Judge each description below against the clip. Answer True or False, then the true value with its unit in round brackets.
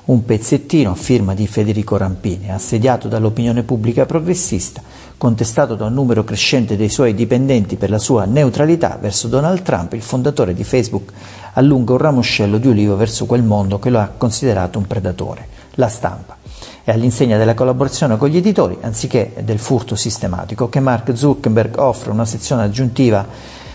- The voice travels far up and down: False (3.6 semitones)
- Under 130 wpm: False (160 wpm)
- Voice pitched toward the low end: True (115 Hz)